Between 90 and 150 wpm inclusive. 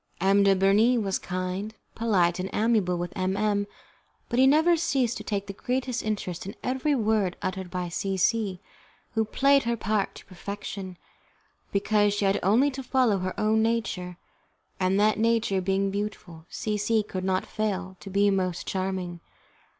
No: average, 170 wpm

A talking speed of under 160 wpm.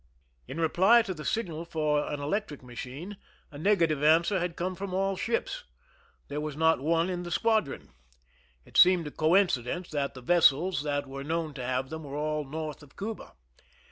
No: average, 185 wpm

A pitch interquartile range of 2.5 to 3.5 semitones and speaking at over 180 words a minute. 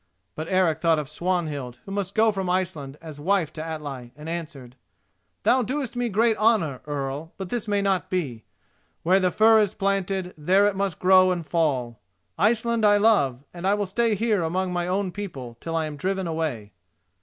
No: average, 4.8 semitones; average, 190 wpm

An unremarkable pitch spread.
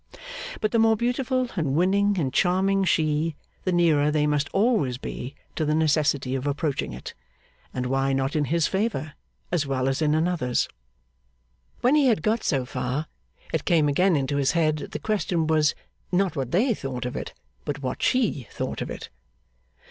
No: wide, 5.8 semitones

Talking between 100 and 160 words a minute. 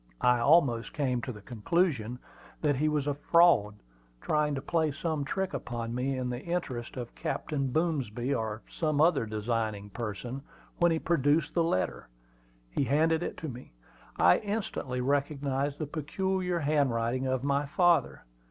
Yes: average, 155 wpm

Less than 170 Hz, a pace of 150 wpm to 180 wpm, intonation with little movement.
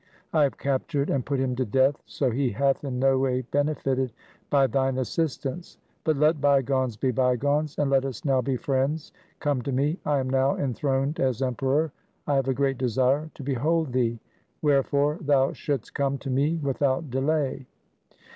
Yes: low, 135 Hz; average, 175 wpm; narrow, 1.7 semitones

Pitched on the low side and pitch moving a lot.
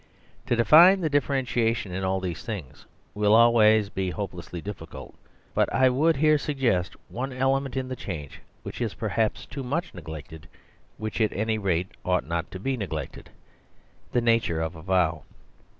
Yes: low, 110 Hz; wide, 6.3 semitones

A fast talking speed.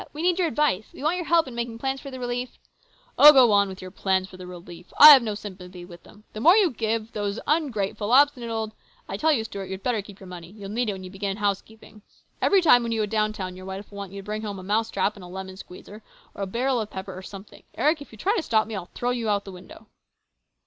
Yes: fast, 275 wpm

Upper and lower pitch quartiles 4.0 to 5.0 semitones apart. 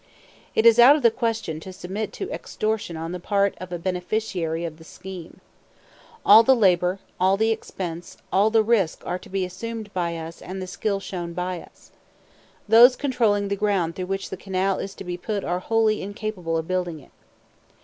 No: average, 3.6 semitones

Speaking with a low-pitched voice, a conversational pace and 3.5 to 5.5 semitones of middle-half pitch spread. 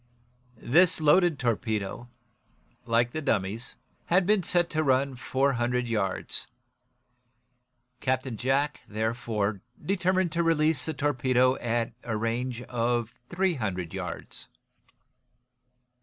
No: low, 125 Hz; slow, 110 wpm; average, 5.1 semitones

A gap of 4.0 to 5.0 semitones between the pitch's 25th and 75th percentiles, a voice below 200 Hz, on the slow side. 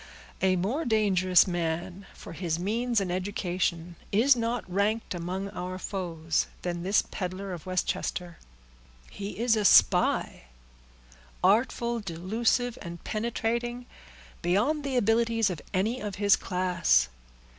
Yes: average, 4.4 semitones; high, 190 Hz; slow, 120 wpm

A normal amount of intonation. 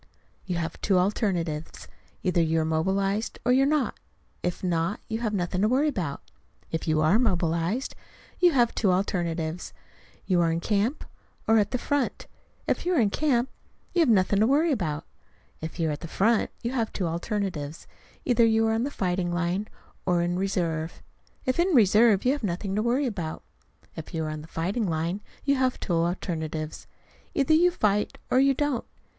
No: wide, 6.0 semitones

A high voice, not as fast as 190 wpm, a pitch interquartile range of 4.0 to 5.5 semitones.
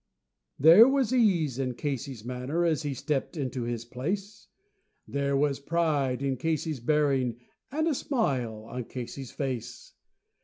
No: medium, 140 Hz; average, 140 wpm; average, 4.4 semitones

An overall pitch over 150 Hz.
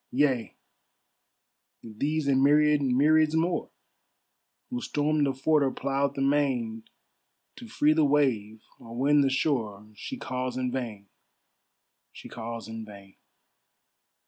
No: low, 135 Hz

